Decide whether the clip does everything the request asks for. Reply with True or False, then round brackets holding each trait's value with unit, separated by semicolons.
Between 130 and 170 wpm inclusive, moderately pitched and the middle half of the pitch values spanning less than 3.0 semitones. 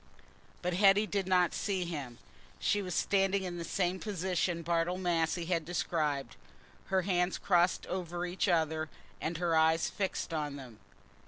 True (155 wpm; 175 Hz; 2.5 semitones)